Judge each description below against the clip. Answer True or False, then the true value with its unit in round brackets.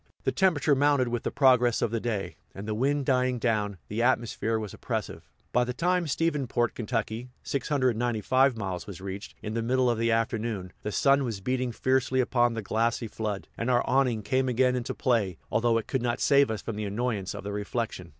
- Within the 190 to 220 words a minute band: True (200 wpm)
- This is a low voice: True (120 Hz)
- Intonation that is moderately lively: True (3.0 semitones)